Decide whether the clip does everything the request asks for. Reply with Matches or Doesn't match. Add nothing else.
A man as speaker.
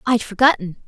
Doesn't match